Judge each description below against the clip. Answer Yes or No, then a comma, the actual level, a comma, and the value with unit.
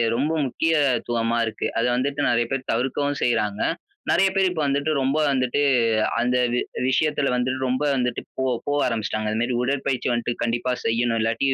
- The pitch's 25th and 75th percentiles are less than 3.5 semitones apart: Yes, average, 3.0 semitones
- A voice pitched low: Yes, low, 125 Hz